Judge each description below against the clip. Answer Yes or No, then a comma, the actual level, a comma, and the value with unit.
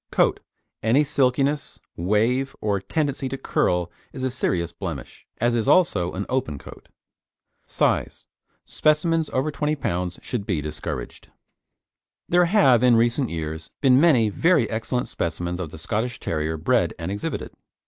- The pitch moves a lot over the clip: Yes, wide, 7.5 semitones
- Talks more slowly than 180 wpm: Yes, average, 150 wpm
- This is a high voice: No, low, 115 Hz